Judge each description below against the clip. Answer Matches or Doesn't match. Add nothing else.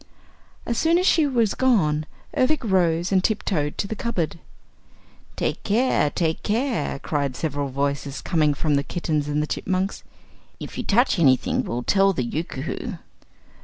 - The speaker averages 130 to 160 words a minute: Matches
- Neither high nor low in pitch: Matches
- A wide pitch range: Matches